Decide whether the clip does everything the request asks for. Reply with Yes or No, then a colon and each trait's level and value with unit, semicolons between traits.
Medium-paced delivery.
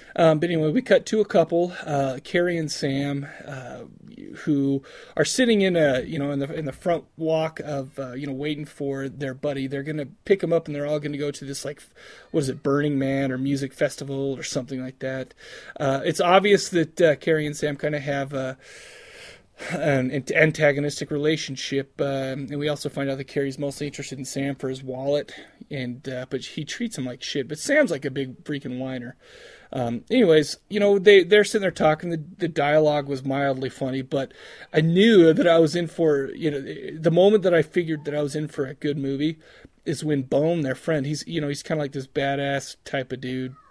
No: fast, 220 wpm